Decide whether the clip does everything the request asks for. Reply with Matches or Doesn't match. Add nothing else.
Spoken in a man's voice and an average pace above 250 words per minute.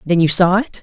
Doesn't match